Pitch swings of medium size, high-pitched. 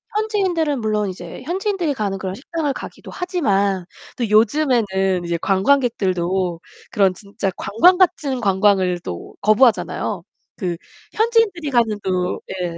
No: wide, 8.1 semitones; high, 215 Hz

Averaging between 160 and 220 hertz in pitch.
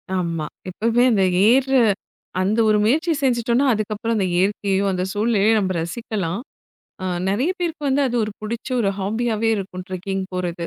Yes: high, 215 Hz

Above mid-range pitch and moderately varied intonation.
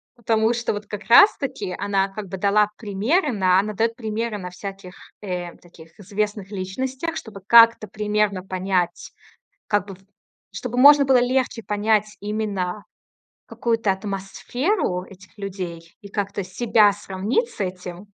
Yes: high, 205 Hz; average, 3.1 semitones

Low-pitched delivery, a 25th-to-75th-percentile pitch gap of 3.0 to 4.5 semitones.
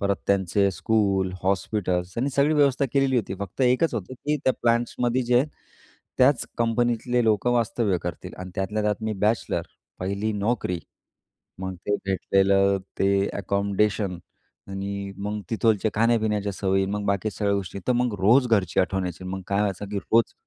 Yes: low, 105 Hz; average, 3.3 semitones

